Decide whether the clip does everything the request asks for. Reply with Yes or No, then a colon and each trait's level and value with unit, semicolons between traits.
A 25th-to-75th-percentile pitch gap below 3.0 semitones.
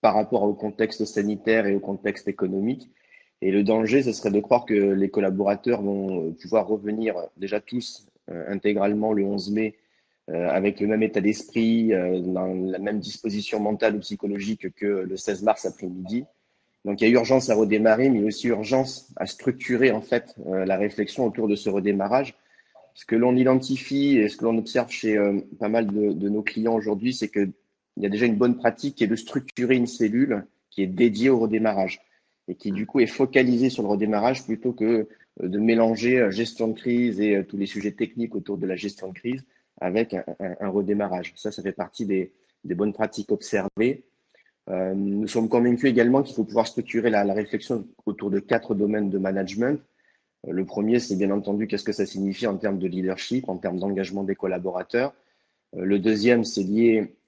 Yes: narrow, 2.5 semitones